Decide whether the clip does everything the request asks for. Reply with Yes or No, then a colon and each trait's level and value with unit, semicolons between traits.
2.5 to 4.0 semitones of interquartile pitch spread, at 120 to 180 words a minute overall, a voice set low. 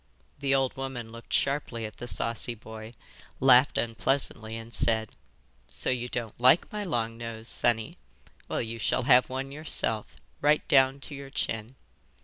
Yes: average, 3.1 semitones; average, 155 wpm; low, 120 Hz